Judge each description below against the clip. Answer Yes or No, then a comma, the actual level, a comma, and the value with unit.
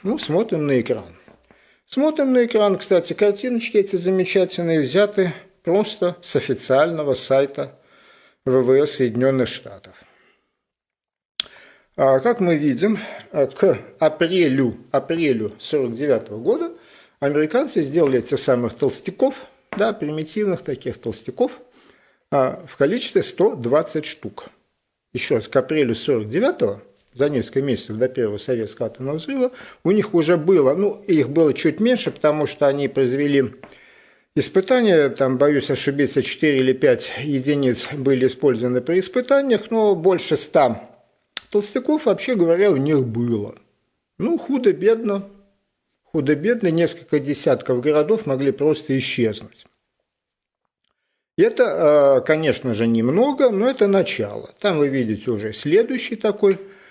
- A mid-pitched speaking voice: Yes, medium, 165 Hz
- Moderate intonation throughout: No, wide, 7.4 semitones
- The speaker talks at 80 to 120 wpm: Yes, average, 115 wpm